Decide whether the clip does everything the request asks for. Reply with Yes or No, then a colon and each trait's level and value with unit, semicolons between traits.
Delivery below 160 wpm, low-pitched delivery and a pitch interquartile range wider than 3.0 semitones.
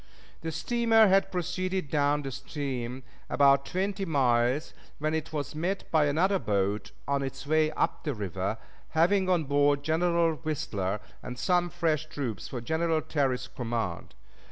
No: average, 150 wpm; medium, 150 Hz; average, 4.6 semitones